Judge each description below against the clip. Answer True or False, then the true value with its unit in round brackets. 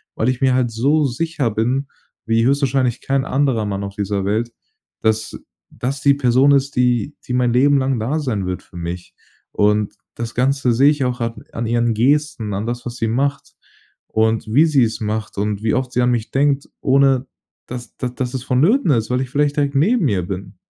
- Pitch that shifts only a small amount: False (3.7 semitones)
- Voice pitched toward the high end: False (125 Hz)